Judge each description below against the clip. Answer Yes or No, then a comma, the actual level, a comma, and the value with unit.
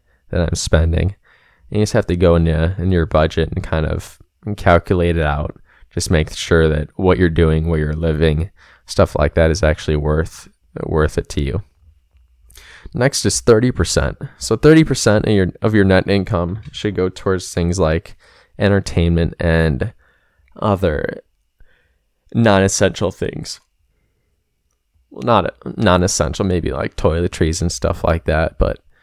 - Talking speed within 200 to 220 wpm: No, average, 155 wpm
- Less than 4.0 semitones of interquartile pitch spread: Yes, average, 3.3 semitones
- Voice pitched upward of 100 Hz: No, very low, 85 Hz